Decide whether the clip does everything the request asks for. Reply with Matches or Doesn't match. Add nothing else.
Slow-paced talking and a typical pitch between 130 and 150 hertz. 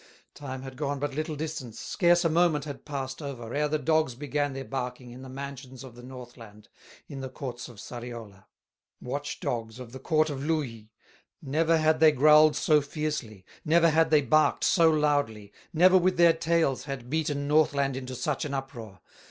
Doesn't match